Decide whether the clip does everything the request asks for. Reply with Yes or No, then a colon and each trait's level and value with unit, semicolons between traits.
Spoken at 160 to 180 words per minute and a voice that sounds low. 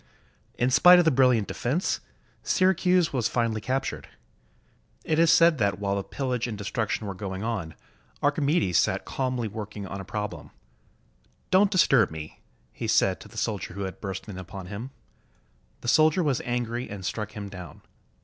Yes: average, 170 wpm; low, 115 Hz